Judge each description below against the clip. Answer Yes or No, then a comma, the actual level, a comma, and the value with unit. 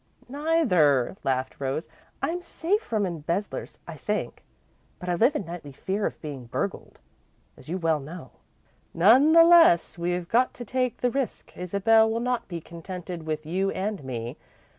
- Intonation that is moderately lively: No, wide, 7.3 semitones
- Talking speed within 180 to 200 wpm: No, average, 160 wpm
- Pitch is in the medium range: Yes, medium, 180 Hz